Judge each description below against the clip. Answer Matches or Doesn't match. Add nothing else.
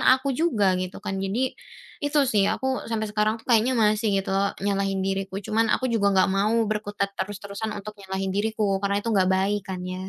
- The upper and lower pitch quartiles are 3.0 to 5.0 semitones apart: Doesn't match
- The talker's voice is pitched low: Doesn't match